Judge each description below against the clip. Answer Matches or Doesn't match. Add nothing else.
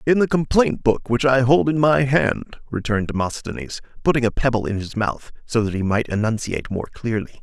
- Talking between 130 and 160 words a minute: Doesn't match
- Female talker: Doesn't match